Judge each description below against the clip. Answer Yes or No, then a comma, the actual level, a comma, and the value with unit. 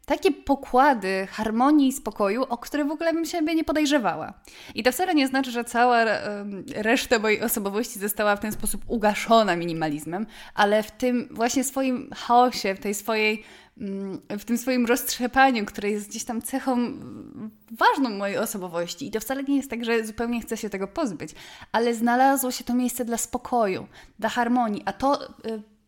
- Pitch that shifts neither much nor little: Yes, average, 3.6 semitones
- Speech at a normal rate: No, fast, 170 wpm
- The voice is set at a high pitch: Yes, high, 235 Hz